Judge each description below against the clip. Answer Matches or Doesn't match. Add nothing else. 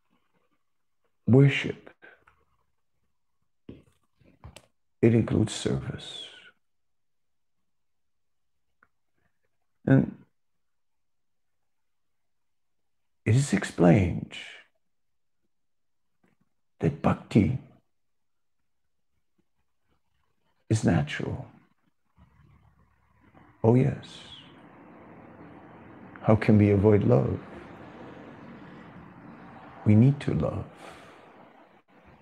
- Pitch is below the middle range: Matches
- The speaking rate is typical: Doesn't match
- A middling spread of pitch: Matches